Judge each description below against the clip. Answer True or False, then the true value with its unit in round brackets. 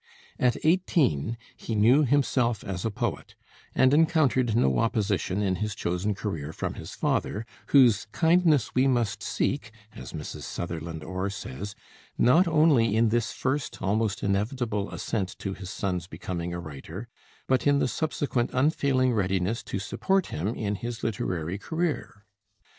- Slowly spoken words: False (145 wpm)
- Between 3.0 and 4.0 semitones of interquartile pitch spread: False (5.5 semitones)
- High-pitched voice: False (110 Hz)